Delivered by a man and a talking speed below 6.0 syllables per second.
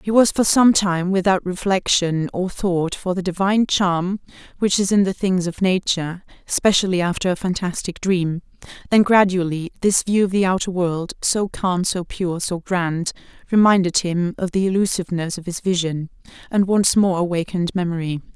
No: female; 4.9 syllables/s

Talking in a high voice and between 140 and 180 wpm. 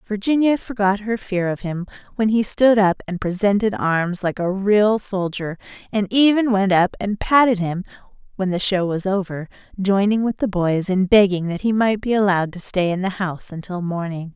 No: high, 195 Hz; average, 195 wpm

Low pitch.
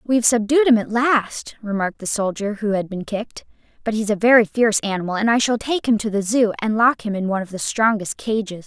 No: high, 215 Hz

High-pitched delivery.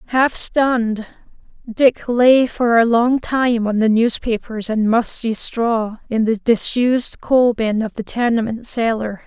Yes: high, 230 Hz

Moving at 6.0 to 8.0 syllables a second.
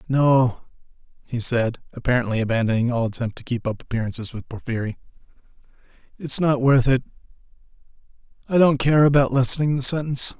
Yes: 6.1 syllables/s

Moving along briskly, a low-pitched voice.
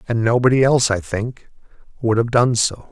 No: average, 185 wpm; low, 120 Hz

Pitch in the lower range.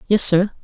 No: high, 190 Hz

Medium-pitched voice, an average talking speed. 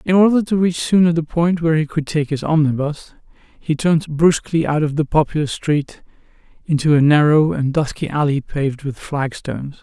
Yes: medium, 155 Hz; average, 185 wpm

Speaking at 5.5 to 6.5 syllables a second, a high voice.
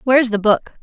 Yes: 6.1 syllables/s; high, 235 Hz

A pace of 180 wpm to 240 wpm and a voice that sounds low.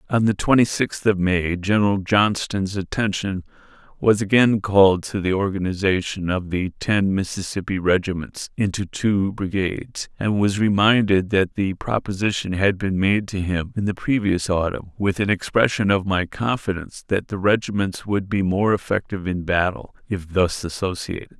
No: average, 155 wpm; low, 100 Hz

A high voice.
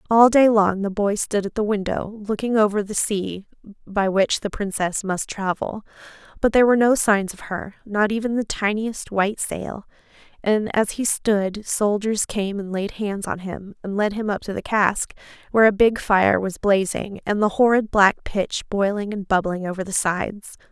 Yes: high, 205 Hz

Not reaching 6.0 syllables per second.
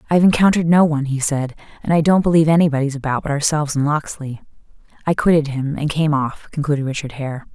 No: 6.8 syllables/s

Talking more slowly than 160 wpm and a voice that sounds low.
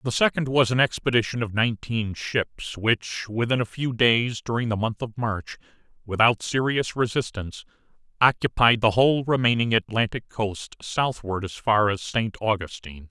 Yes: average, 150 wpm; low, 115 Hz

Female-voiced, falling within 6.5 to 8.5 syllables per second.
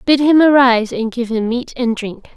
No: female; 5.1 syllables/s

